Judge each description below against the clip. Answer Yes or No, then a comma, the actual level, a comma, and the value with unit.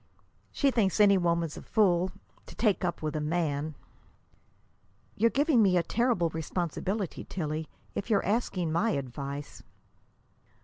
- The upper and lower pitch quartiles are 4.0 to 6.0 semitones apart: Yes, average, 5.2 semitones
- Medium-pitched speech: Yes, medium, 175 Hz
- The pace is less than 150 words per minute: Yes, slow, 135 wpm